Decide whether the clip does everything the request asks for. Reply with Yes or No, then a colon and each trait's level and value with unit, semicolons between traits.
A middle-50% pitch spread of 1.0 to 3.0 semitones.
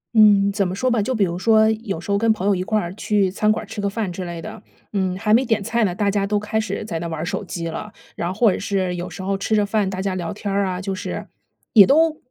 Yes: narrow, 2.6 semitones